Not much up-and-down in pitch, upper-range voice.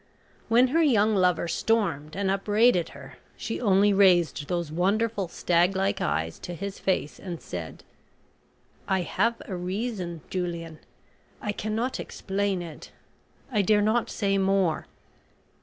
No: average, 3.3 semitones; high, 195 Hz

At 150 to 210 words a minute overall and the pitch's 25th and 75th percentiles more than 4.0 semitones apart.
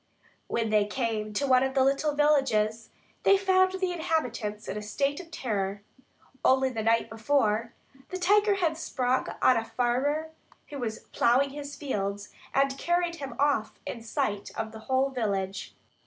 Yes: average, 165 wpm; average, 5.1 semitones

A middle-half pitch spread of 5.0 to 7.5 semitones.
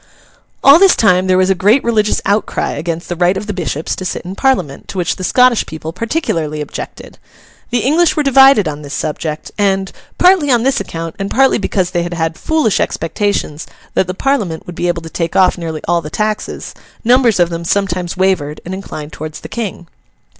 Yes: average, 5.3 semitones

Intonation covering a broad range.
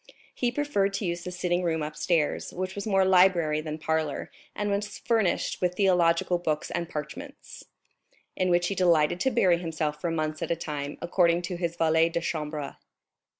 No: average, 2.9 semitones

